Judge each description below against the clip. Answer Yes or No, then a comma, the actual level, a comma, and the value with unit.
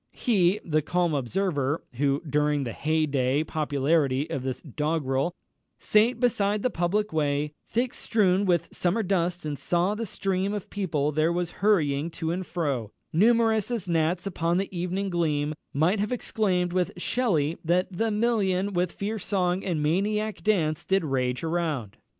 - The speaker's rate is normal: Yes, average, 160 wpm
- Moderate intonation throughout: Yes, average, 4.9 semitones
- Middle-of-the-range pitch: Yes, medium, 175 Hz